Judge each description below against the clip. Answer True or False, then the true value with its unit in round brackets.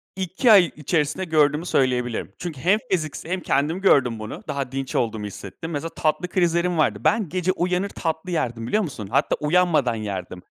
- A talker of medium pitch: True (155 Hz)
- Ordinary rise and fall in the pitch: False (5.9 semitones)